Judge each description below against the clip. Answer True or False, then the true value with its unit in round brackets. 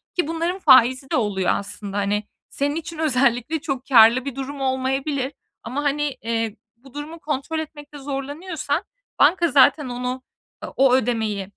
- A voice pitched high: True (270 Hz)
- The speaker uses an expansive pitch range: False (3.3 semitones)